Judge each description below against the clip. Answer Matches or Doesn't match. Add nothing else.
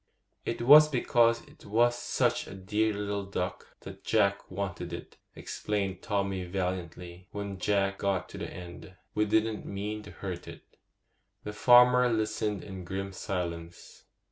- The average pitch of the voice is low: Matches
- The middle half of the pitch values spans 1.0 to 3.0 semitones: Matches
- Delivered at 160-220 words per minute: Doesn't match